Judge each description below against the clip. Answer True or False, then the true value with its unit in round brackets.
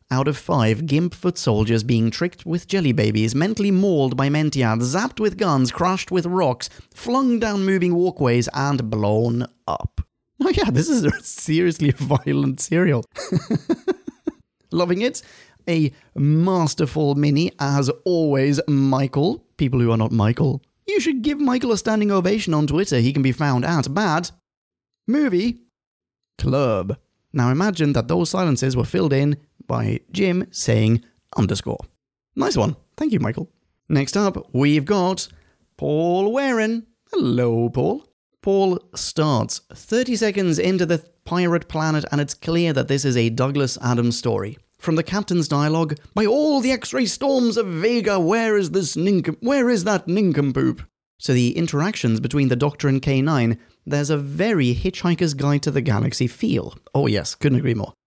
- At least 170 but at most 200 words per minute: False (155 wpm)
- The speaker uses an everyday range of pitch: False (6.4 semitones)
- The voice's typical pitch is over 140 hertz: True (150 Hz)